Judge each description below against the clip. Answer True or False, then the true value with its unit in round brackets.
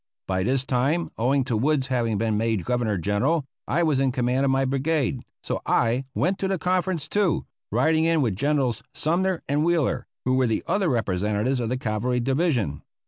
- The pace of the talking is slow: False (190 wpm)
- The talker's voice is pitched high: False (130 Hz)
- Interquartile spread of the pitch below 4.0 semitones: False (5.3 semitones)